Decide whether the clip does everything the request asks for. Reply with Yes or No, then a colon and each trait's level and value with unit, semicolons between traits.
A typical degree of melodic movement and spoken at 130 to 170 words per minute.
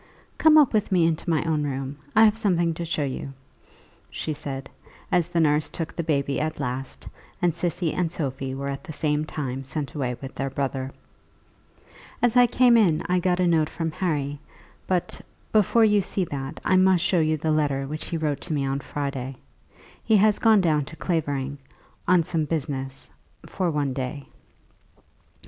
No: average, 4.3 semitones; average, 185 wpm